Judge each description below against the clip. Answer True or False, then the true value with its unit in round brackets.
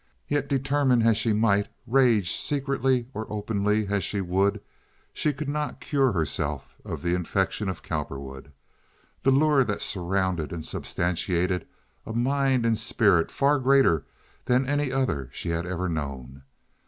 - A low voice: True (105 Hz)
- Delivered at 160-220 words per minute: False (145 wpm)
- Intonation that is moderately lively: False (7.2 semitones)